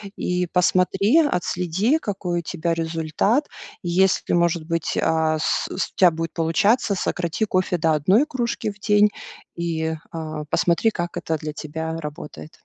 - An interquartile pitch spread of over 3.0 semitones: Yes, average, 3.4 semitones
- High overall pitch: No, medium, 175 Hz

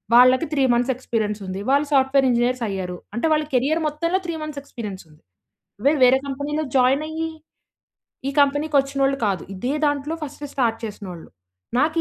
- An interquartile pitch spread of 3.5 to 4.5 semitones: Yes, average, 3.9 semitones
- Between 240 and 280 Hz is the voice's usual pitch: Yes, very high, 270 Hz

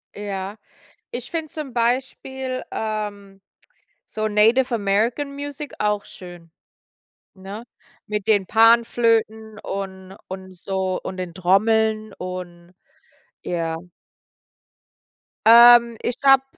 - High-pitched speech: Yes, high, 215 Hz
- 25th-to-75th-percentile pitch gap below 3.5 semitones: No, average, 3.8 semitones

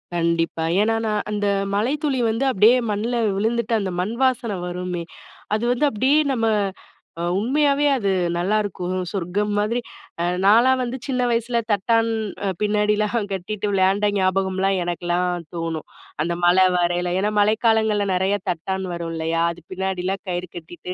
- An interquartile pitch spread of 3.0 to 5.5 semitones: Yes, average, 4.1 semitones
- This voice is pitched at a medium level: No, high, 205 Hz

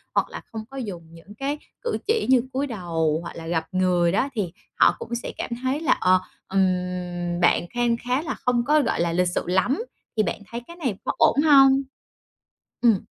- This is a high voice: Yes, high, 215 Hz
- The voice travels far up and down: Yes, wide, 7.1 semitones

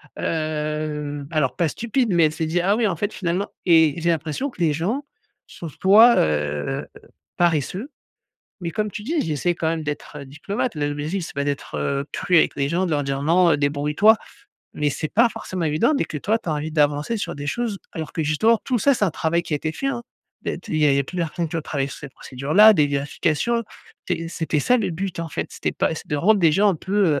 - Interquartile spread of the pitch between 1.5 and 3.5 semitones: No, average, 5.0 semitones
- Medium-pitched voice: Yes, medium, 165 Hz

